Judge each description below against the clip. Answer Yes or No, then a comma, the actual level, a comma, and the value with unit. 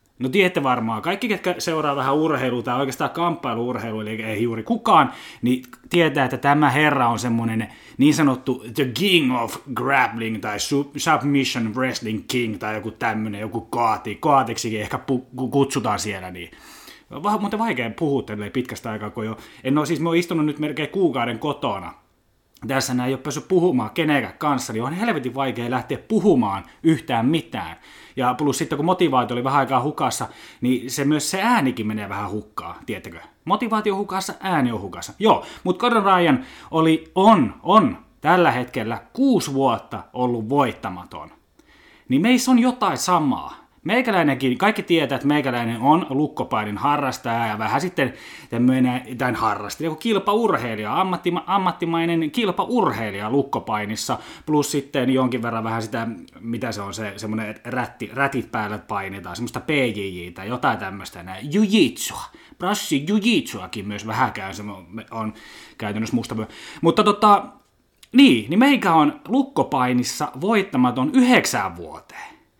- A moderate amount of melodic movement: No, wide, 6.8 semitones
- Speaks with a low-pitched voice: Yes, low, 130 Hz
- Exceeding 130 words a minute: Yes, average, 150 wpm